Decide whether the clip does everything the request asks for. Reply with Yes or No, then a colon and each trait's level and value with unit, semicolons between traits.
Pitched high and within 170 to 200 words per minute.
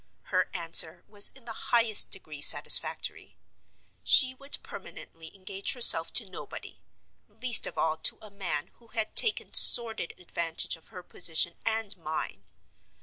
No: high, 195 Hz; average, 140 wpm